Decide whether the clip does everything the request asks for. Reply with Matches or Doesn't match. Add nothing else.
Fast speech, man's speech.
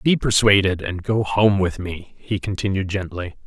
Doesn't match